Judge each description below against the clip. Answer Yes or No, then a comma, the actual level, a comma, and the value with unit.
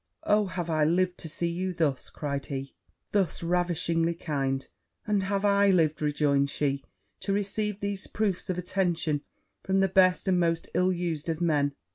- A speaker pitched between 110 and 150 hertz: No, medium, 175 Hz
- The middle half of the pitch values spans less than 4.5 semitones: Yes, average, 3.8 semitones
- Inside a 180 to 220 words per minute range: No, average, 170 wpm